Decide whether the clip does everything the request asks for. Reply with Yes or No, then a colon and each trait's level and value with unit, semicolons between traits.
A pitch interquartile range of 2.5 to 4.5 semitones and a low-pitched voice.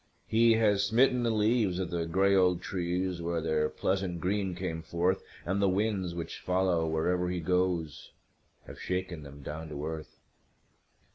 Yes: average, 2.8 semitones; very low, 90 Hz